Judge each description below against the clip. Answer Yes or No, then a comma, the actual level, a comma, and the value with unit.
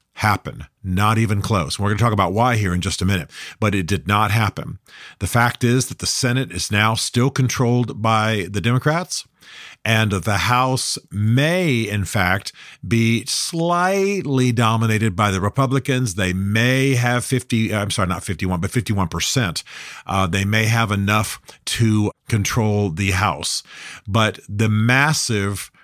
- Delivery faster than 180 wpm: No, average, 155 wpm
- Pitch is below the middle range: Yes, low, 110 Hz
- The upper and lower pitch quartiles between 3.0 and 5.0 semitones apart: Yes, average, 3.8 semitones